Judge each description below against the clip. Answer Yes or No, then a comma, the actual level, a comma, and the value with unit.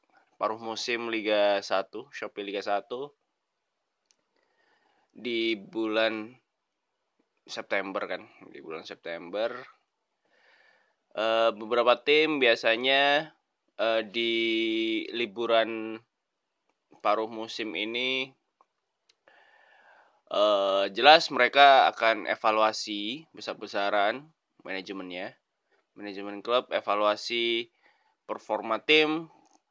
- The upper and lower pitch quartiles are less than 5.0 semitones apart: Yes, average, 4.1 semitones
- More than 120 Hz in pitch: No, low, 115 Hz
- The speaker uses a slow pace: Yes, slow, 65 wpm